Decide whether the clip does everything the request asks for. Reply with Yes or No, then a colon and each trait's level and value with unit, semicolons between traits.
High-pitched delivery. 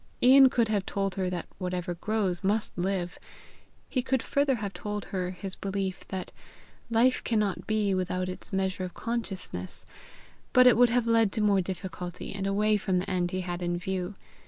Yes: high, 195 Hz